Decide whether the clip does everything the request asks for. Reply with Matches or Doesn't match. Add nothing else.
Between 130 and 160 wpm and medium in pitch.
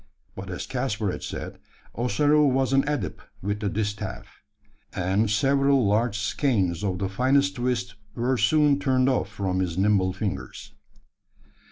Doesn't match